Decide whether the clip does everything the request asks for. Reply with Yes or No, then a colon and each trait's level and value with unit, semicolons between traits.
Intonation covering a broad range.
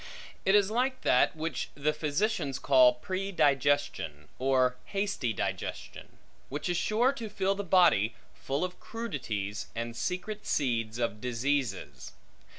Yes: wide, 8.0 semitones